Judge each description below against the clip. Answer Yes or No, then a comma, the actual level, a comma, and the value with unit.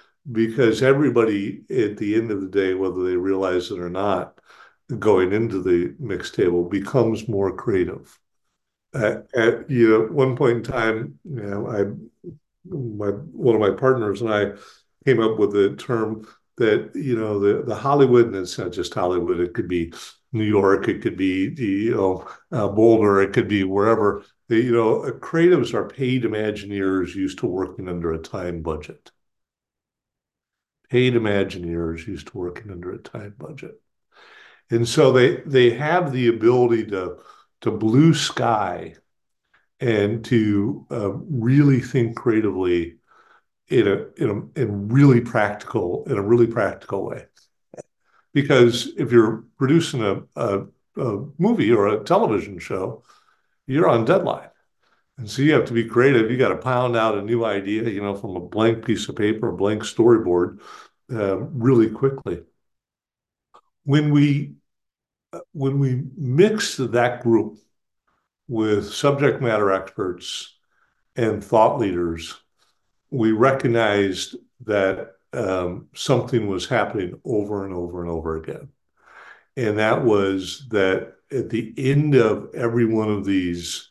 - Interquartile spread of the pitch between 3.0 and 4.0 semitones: No, average, 4.4 semitones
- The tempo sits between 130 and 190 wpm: Yes, average, 145 wpm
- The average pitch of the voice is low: Yes, low, 110 Hz